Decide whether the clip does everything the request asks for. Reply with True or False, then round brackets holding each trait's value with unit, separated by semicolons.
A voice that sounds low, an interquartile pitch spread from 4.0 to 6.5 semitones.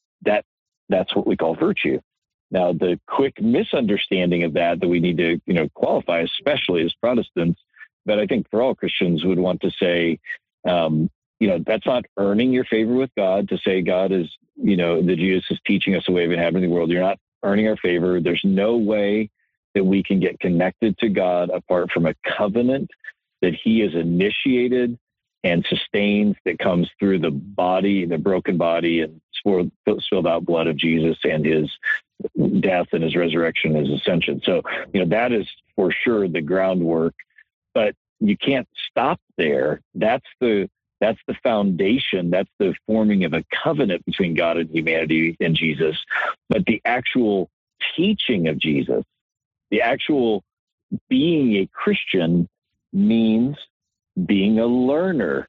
True (90 Hz; 4.5 semitones)